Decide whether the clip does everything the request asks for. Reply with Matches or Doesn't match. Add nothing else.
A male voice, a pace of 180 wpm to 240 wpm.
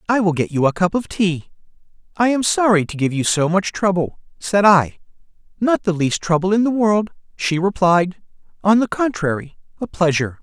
Matches